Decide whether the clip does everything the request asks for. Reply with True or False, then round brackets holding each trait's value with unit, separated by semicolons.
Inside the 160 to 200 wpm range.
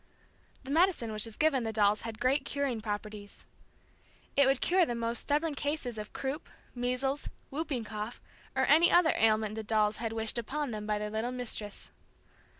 True (175 wpm)